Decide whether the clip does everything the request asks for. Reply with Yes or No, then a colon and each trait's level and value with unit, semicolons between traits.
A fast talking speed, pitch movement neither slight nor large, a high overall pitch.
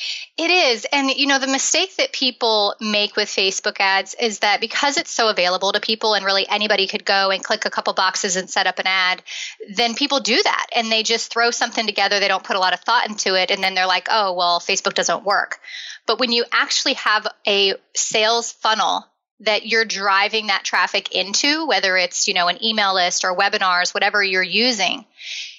Yes: fast, 210 wpm; average, 3.4 semitones; high, 210 Hz